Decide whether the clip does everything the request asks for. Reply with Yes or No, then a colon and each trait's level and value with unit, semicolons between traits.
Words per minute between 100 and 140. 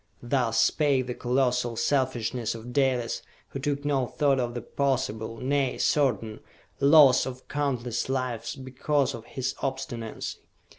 Yes: slow, 135 wpm